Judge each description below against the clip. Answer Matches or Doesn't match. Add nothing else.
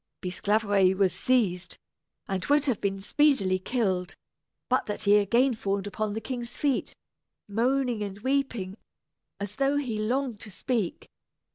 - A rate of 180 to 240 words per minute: Doesn't match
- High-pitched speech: Matches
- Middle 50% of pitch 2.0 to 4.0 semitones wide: Doesn't match